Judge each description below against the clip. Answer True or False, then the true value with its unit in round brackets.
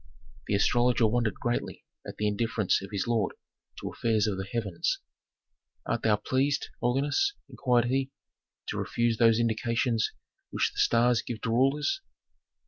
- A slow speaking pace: False (145 wpm)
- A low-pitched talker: True (115 Hz)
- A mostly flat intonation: True (2.1 semitones)